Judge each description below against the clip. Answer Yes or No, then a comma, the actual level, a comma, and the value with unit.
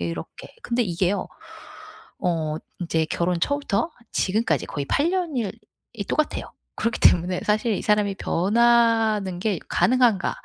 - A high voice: Yes, high, 205 Hz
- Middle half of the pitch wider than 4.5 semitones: Yes, average, 5.1 semitones